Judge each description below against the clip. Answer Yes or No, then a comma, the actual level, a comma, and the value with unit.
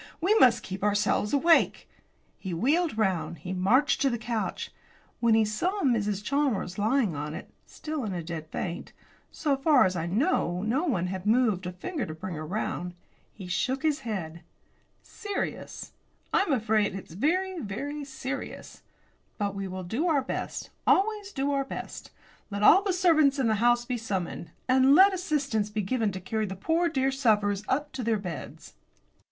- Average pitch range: No, wide, 6.9 semitones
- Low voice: No, high, 230 Hz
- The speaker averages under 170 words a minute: No, average, 180 wpm